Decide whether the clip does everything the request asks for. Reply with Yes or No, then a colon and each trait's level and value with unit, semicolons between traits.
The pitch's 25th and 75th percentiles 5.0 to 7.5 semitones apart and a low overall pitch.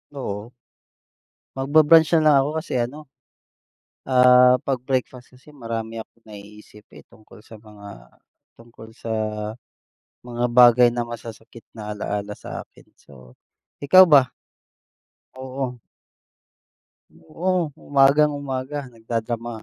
No: average, 3.6 semitones; low, 125 Hz